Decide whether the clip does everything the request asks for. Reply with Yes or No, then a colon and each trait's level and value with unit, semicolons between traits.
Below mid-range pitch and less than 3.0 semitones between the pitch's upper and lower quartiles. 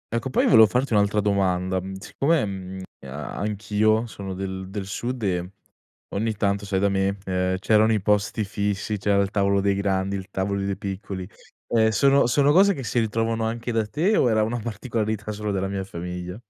Yes: low, 100 Hz; narrow, 2.5 semitones